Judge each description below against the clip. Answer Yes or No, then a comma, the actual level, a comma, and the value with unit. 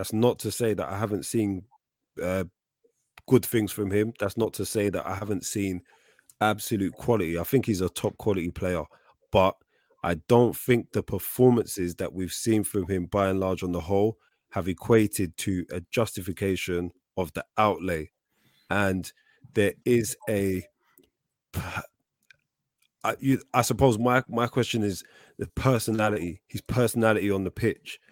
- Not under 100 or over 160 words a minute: Yes, average, 155 wpm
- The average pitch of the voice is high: No, low, 105 Hz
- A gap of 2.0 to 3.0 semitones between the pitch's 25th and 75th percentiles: No, average, 3.7 semitones